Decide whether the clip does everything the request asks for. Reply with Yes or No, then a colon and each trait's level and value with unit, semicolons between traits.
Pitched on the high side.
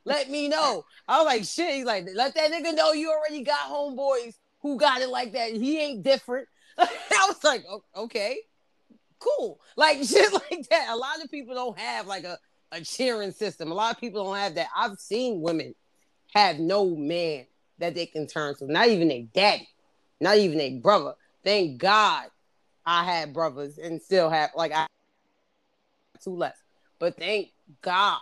Yes: high, 230 Hz